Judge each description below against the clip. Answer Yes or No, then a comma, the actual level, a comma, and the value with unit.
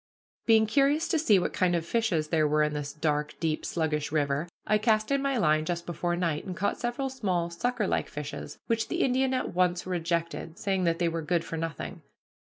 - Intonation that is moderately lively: No, wide, 5.7 semitones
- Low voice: No, medium, 175 Hz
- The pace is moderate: No, fast, 210 wpm